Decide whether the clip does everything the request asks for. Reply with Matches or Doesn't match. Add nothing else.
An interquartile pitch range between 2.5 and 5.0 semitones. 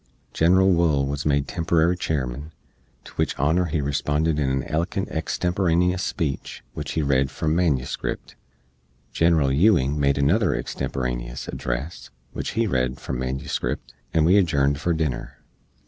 Matches